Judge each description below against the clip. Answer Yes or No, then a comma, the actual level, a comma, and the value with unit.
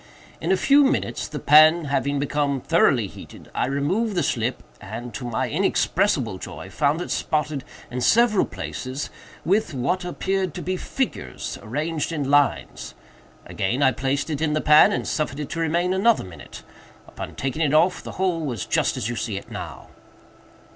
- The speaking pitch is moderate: Yes, medium, 150 Hz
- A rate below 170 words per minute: No, average, 175 wpm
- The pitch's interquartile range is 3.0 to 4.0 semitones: No, average, 5.1 semitones